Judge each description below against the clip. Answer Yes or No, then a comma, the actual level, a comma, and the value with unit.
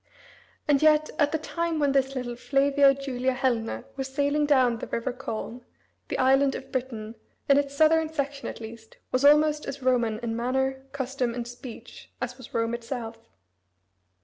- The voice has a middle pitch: No, very high, 265 Hz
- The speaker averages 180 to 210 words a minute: No, average, 170 wpm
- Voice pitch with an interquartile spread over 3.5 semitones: No, average, 2.7 semitones